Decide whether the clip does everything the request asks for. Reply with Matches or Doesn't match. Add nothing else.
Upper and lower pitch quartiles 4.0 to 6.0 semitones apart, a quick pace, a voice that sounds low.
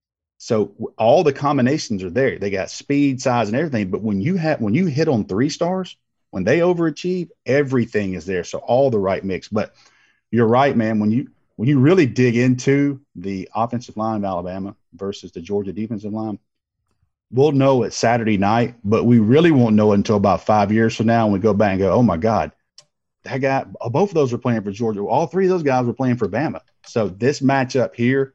Matches